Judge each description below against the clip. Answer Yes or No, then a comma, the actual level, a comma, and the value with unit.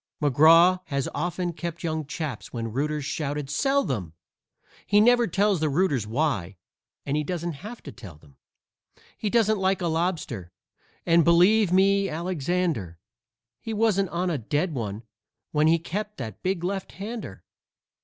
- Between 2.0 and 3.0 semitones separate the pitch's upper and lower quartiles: No, wide, 5.5 semitones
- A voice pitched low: No, medium, 165 Hz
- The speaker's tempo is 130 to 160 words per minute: Yes, average, 150 wpm